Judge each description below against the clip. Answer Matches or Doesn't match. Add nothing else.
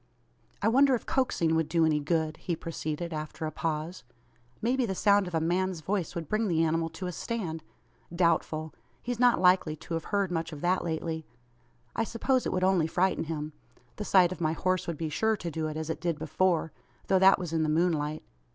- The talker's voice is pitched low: Doesn't match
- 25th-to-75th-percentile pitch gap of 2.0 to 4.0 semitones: Matches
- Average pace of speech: Doesn't match